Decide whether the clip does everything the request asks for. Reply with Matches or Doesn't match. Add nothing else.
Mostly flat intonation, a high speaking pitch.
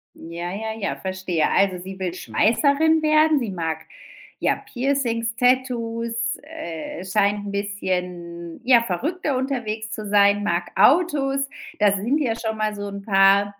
Doesn't match